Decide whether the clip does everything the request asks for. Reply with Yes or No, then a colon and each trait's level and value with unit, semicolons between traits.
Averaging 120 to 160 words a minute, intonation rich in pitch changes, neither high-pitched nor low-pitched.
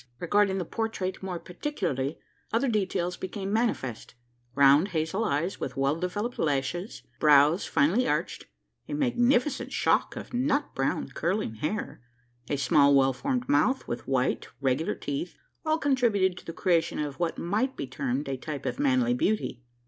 Yes: average, 155 wpm; wide, 8.2 semitones; medium, 180 Hz